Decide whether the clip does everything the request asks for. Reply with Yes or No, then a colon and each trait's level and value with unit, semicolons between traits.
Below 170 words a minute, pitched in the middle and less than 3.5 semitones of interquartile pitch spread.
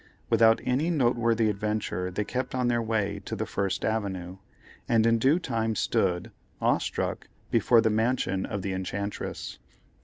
No: average, 155 wpm; low, 110 Hz; average, 3.0 semitones